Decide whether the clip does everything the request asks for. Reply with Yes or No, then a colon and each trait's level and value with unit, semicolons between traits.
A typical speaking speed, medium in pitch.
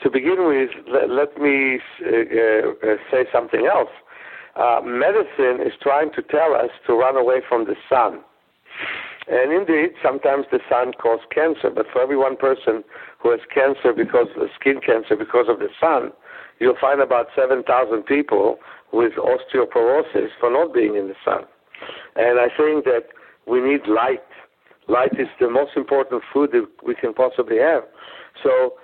Yes: average, 165 wpm; medium, 155 Hz